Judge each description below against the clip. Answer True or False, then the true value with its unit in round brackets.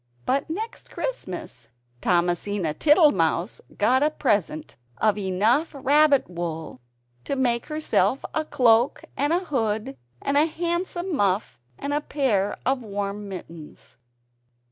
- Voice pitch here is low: False (235 Hz)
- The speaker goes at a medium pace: False (120 wpm)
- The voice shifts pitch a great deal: True (7.8 semitones)